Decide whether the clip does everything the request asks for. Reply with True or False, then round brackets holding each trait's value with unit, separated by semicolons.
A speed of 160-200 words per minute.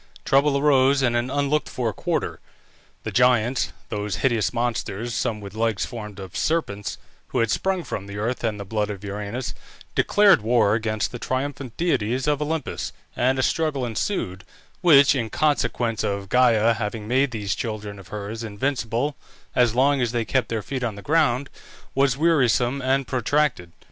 True (170 wpm)